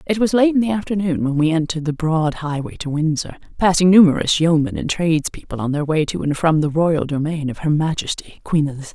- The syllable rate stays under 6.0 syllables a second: No, 6.1 syllables/s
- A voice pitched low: No, medium, 160 Hz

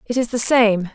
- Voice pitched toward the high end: Yes, high, 230 Hz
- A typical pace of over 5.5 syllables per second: No, 4.9 syllables/s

